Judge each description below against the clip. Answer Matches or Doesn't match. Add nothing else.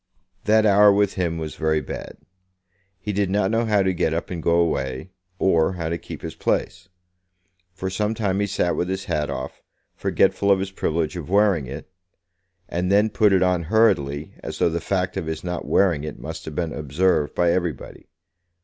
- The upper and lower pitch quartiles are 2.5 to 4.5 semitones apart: Matches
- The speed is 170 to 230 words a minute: Matches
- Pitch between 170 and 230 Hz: Doesn't match